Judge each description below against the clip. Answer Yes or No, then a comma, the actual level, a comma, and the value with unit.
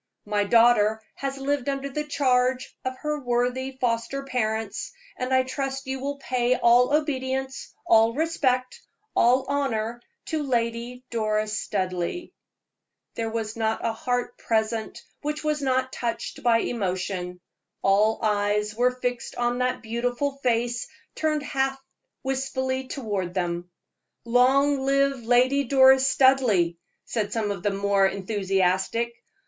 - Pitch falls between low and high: No, high, 245 Hz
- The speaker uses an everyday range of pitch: Yes, average, 3.4 semitones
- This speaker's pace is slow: Yes, slow, 130 wpm